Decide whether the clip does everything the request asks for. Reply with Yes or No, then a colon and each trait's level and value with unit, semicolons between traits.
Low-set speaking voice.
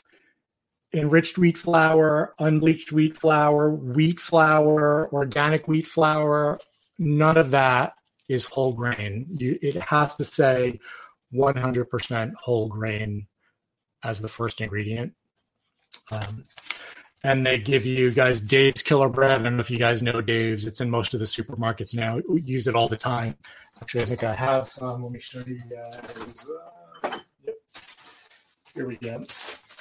Yes: low, 130 Hz